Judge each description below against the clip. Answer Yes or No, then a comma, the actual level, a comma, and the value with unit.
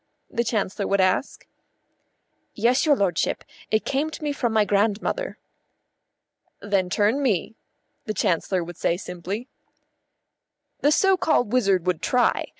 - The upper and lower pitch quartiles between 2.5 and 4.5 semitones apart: No, average, 5.2 semitones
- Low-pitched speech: No, high, 210 Hz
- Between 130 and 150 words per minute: Yes, slow, 135 wpm